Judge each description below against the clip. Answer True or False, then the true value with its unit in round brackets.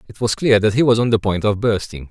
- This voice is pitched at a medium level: False (110 Hz)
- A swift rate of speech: True (315 wpm)